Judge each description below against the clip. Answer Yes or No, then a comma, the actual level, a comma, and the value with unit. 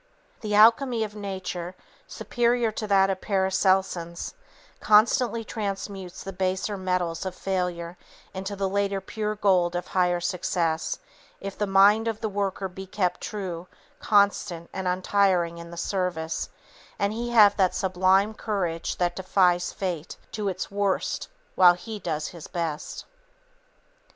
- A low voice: No, high, 190 Hz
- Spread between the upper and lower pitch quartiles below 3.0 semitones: Yes, narrow, 2.5 semitones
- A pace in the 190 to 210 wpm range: No, average, 140 wpm